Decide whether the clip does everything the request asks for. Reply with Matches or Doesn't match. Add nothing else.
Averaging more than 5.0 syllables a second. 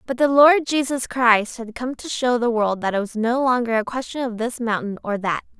Matches